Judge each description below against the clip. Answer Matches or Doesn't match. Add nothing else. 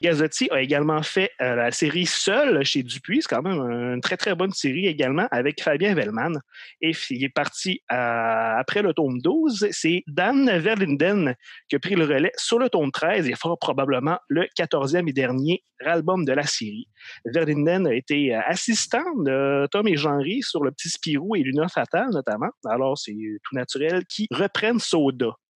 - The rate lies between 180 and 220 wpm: Matches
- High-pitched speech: Doesn't match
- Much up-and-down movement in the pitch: Matches